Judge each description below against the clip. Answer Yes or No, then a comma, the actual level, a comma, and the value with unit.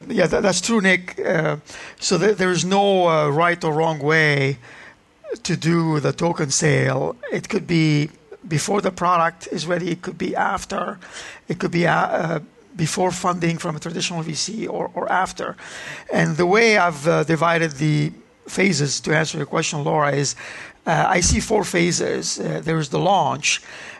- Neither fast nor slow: Yes, average, 170 wpm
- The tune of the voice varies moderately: Yes, average, 3.0 semitones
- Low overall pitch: No, medium, 170 Hz